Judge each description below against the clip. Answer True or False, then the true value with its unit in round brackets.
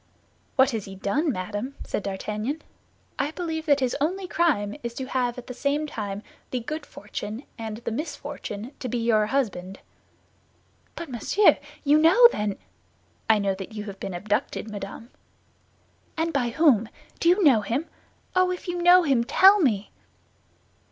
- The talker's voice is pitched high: True (250 Hz)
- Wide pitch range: True (6.5 semitones)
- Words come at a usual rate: True (165 wpm)